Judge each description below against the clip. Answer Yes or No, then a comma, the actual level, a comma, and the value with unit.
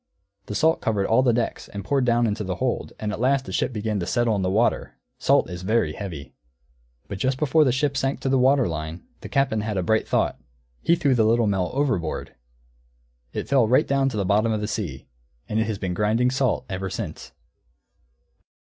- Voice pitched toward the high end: No, low, 110 Hz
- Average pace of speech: No, fast, 215 wpm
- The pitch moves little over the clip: No, average, 4.6 semitones